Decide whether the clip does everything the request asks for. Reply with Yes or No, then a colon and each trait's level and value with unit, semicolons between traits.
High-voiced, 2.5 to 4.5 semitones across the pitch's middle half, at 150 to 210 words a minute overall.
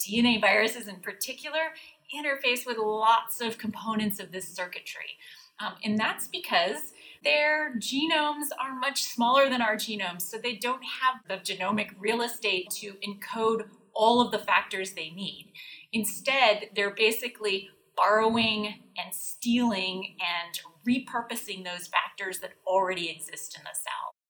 No: high, 220 Hz; average, 3.9 semitones; average, 140 wpm